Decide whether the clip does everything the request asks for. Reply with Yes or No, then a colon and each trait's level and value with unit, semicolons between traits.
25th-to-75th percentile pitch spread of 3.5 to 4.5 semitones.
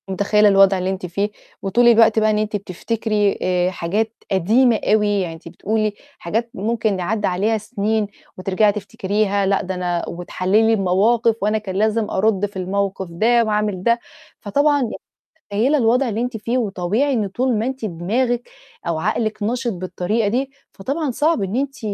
No: average, 3.1 semitones